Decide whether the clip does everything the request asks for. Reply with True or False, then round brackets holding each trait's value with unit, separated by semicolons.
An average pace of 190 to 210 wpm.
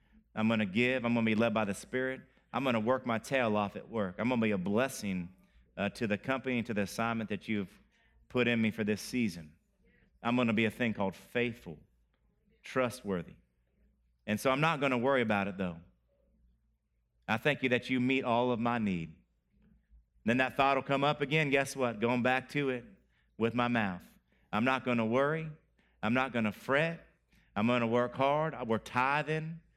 True (195 wpm)